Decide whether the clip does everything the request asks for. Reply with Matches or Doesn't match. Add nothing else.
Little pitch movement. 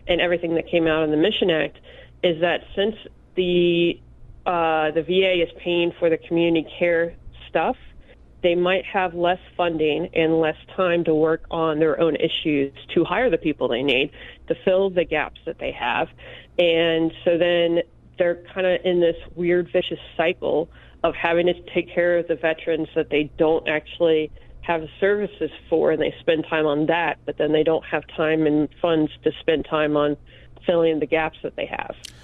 Matches